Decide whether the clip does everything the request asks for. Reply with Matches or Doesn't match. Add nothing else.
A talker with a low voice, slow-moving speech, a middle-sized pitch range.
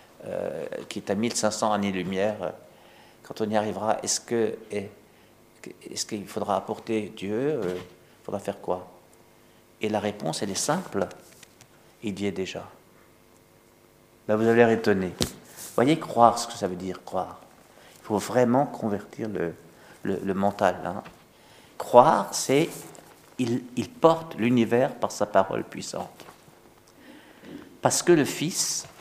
Matches